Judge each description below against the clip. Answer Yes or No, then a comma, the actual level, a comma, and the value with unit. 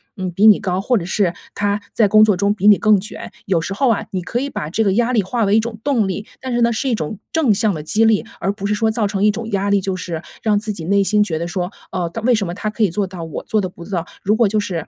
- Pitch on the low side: No, high, 205 Hz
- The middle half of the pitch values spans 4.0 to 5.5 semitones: No, average, 2.8 semitones